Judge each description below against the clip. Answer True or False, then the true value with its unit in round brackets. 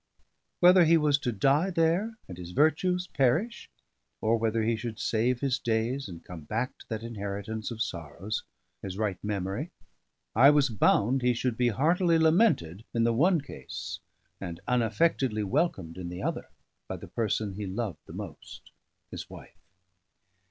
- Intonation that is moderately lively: False (6.4 semitones)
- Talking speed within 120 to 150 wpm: False (160 wpm)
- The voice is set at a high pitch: False (115 Hz)